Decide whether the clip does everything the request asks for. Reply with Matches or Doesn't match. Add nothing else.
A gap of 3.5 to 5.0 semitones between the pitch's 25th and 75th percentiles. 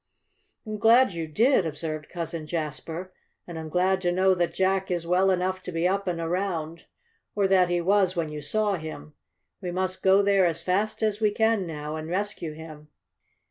Doesn't match